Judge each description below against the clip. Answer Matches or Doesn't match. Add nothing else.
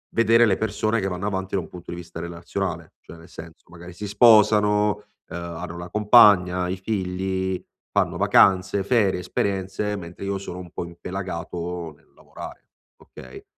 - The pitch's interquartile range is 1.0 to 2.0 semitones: Doesn't match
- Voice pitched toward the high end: Doesn't match